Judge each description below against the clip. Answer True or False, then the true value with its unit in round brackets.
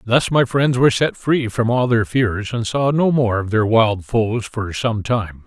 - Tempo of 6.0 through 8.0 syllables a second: False (4.1 syllables/s)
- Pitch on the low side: True (115 Hz)